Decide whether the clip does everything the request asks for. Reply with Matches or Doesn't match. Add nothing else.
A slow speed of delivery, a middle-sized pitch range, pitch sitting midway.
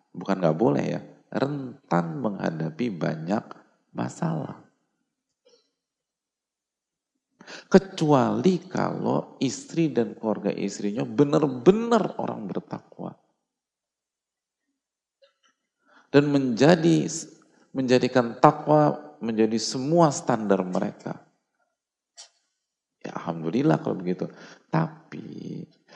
Doesn't match